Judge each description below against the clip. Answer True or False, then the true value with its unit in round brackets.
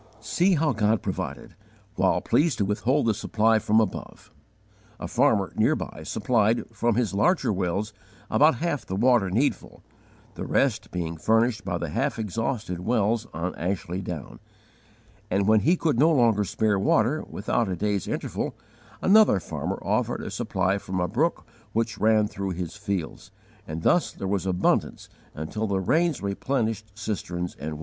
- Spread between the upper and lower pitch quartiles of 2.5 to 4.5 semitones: True (3.8 semitones)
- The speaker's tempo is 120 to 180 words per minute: True (160 wpm)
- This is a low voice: True (105 Hz)